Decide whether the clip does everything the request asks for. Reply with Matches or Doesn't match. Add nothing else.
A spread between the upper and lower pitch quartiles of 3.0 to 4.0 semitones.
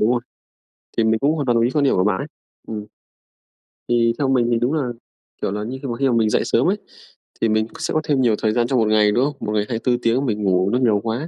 Matches